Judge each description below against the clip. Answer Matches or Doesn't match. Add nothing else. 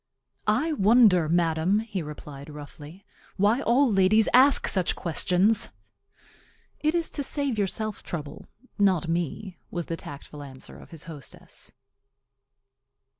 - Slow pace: Matches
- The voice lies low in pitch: Doesn't match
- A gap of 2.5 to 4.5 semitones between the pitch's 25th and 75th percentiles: Doesn't match